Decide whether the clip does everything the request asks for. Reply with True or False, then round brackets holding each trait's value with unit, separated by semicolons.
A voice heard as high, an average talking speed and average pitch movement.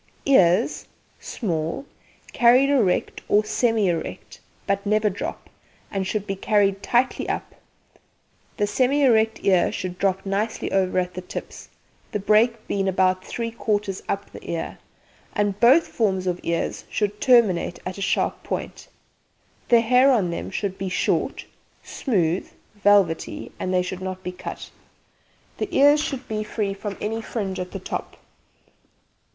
True (200 Hz; 150 wpm; 3.3 semitones)